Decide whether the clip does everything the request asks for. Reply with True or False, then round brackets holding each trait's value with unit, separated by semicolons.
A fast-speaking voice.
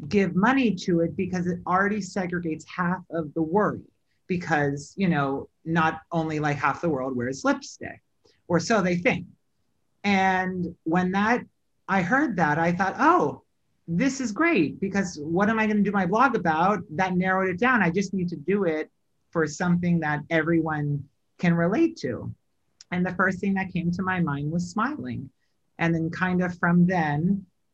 False (180 wpm)